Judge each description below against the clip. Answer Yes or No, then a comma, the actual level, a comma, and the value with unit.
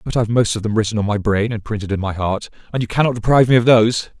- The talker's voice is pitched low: Yes, low, 110 Hz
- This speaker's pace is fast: Yes, fast, 300 wpm